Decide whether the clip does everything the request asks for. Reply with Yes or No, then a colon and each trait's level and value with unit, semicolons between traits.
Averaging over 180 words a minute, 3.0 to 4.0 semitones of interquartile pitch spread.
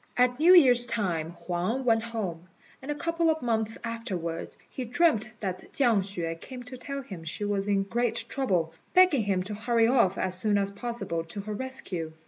No: average, 190 wpm; average, 5.0 semitones